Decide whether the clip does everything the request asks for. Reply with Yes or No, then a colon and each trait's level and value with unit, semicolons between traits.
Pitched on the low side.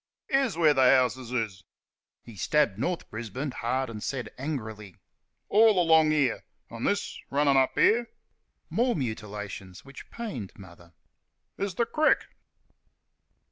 Yes: low, 130 Hz